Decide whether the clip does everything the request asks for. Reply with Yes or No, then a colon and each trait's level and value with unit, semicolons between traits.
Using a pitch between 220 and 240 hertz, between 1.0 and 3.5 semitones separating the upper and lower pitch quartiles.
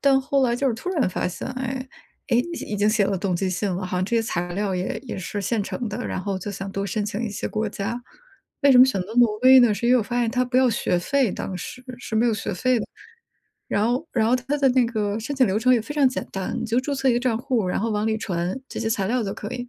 No: high, 225 Hz; average, 4.0 semitones